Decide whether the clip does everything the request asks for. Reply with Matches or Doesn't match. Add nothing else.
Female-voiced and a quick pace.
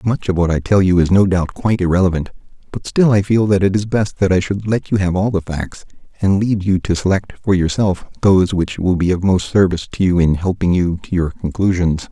Doesn't match